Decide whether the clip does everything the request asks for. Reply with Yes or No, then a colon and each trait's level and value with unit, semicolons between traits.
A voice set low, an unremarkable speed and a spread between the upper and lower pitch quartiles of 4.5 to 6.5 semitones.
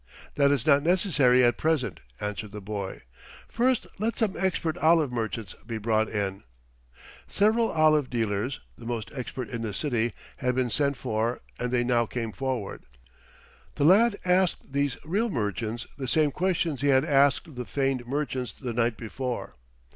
Yes: low, 130 Hz; average, 165 wpm; average, 4.9 semitones